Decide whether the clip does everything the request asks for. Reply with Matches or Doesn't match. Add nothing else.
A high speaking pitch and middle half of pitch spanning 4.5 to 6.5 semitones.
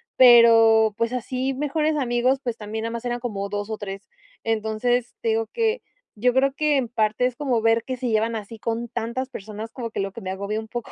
Doesn't match